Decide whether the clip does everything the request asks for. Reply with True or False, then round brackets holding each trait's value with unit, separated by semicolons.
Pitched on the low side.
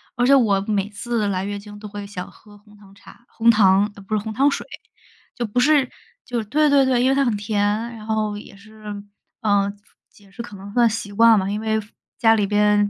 False (210 Hz)